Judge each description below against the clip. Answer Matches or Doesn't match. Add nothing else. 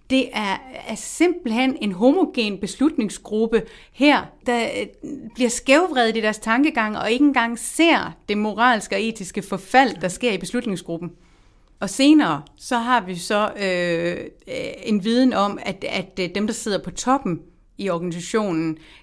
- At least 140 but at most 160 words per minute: Matches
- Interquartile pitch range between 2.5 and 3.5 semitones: Doesn't match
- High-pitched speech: Matches